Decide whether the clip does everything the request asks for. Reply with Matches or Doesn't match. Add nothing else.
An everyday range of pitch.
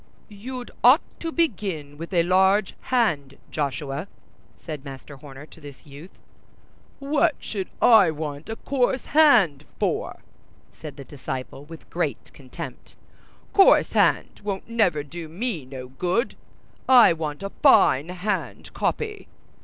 Doesn't match